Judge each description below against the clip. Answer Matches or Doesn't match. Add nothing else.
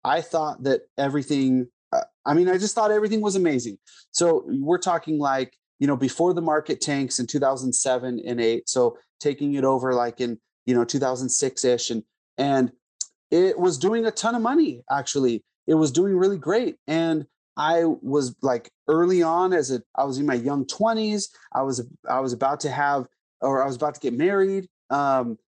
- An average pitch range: Doesn't match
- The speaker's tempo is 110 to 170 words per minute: Doesn't match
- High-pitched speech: Doesn't match